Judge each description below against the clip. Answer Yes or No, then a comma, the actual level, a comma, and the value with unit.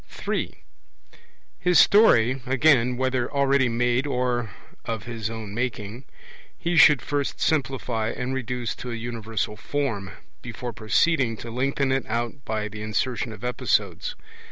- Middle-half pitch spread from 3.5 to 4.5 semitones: No, average, 3.0 semitones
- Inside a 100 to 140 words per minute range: Yes, slow, 135 wpm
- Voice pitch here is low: Yes, low, 120 Hz